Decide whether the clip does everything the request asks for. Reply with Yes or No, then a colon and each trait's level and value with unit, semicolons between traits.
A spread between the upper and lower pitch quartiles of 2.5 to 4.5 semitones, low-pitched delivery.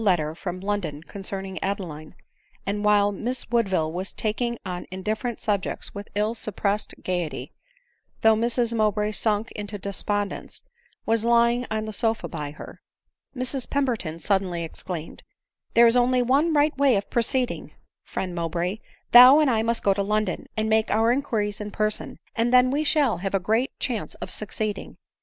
No: average, 3.6 semitones; high, 215 Hz